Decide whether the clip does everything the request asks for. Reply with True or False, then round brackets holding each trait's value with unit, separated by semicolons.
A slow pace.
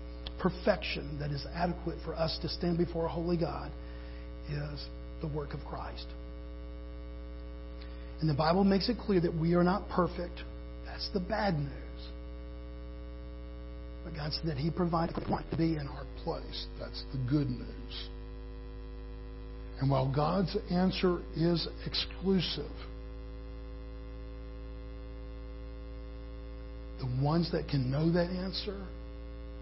True (125 wpm)